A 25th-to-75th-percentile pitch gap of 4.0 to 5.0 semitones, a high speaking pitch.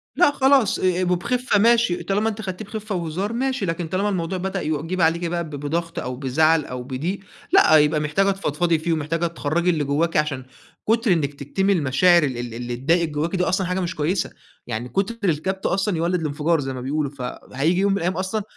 No: average, 4.4 semitones; medium, 170 Hz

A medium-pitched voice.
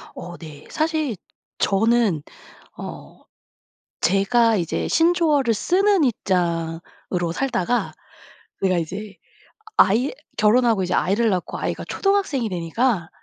No: high, 215 Hz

